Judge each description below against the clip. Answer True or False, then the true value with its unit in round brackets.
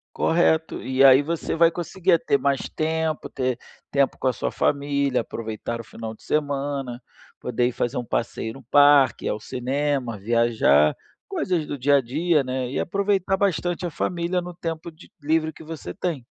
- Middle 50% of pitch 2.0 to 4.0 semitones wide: False (4.7 semitones)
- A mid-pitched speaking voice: True (145 Hz)